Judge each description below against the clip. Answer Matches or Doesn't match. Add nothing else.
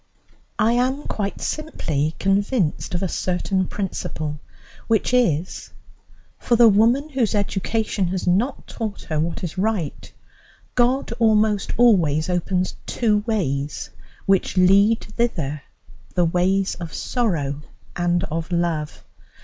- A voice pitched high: Matches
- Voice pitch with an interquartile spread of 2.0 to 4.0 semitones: Doesn't match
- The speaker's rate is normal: Doesn't match